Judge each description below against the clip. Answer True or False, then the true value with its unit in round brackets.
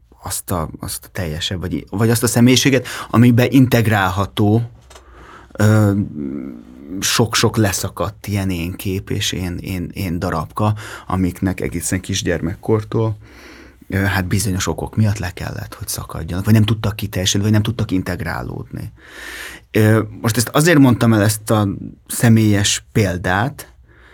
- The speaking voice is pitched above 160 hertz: False (105 Hz)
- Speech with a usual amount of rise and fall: True (3.6 semitones)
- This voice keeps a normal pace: True (130 wpm)